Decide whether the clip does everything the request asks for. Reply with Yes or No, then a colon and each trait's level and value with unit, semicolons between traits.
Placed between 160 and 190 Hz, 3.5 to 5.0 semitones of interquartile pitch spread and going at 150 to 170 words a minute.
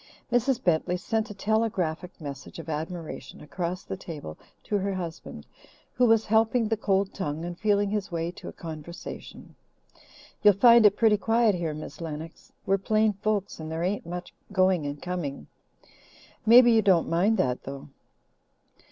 Yes: medium, 185 Hz; average, 4.7 semitones; average, 160 wpm